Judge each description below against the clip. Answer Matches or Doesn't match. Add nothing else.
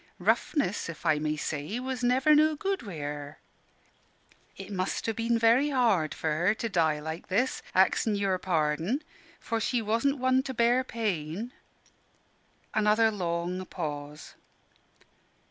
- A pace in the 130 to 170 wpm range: Matches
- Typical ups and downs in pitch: Doesn't match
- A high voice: Matches